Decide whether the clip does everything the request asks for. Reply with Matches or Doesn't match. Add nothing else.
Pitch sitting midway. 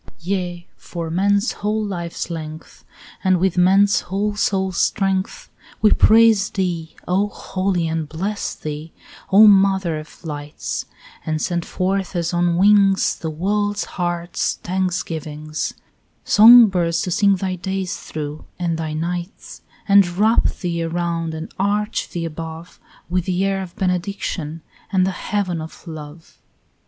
Matches